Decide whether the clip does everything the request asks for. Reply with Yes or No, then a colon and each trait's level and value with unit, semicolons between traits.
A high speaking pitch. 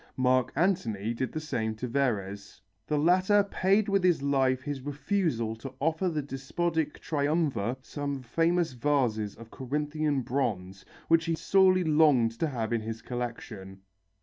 No: medium, 140 Hz